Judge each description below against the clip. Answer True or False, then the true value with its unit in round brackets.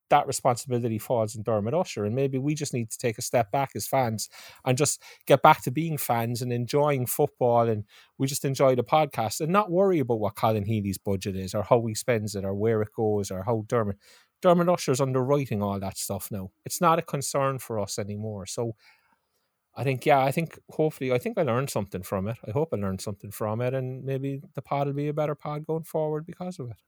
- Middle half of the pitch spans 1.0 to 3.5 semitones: False (5.0 semitones)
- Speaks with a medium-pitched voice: False (125 Hz)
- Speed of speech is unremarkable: False (230 wpm)